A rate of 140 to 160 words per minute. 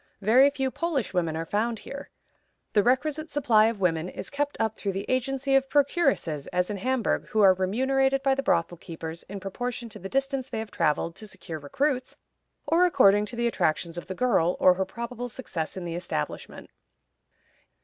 No: average, 190 wpm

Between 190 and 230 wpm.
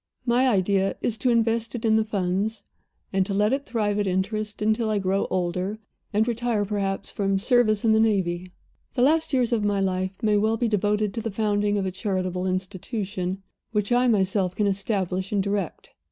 Yes: average, 195 wpm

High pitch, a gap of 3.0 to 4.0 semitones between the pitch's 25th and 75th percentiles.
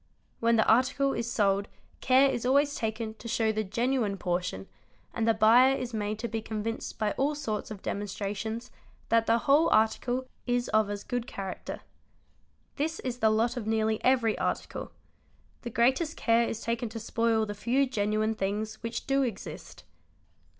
No: high, 225 Hz; narrow, 2.4 semitones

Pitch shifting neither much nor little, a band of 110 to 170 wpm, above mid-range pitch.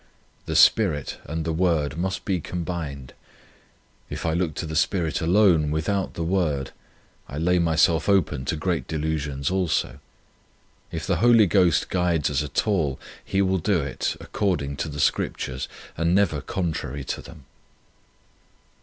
No: average, 3.9 semitones; average, 150 wpm; very low, 80 Hz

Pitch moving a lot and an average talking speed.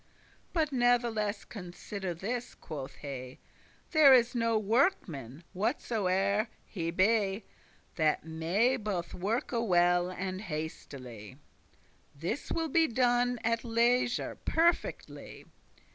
No: wide, 5.7 semitones; slow, 100 wpm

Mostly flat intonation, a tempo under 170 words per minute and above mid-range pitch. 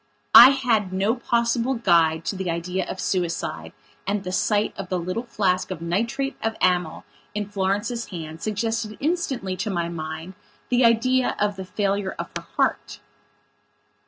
No: average, 4.4 semitones; average, 160 wpm; high, 195 Hz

